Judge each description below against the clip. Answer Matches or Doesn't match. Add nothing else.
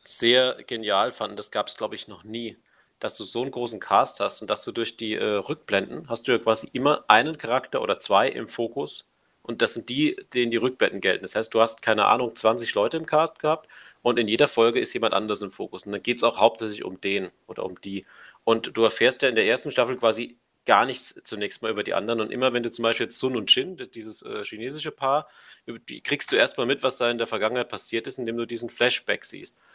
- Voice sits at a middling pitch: Doesn't match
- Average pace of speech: Doesn't match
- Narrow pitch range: Matches